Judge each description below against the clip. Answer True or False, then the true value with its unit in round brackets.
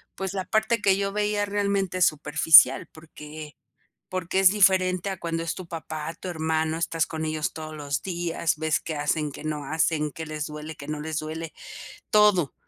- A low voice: False (160 Hz)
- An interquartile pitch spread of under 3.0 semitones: False (3.5 semitones)